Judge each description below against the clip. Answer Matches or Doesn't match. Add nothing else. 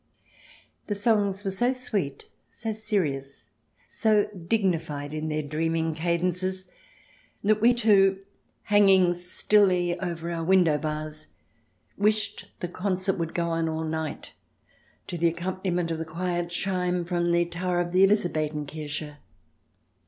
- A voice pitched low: Doesn't match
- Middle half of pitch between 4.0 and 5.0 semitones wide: Doesn't match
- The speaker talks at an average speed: Doesn't match